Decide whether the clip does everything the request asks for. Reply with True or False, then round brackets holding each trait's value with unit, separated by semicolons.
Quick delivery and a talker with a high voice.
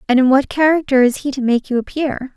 True (255 wpm; 265 Hz)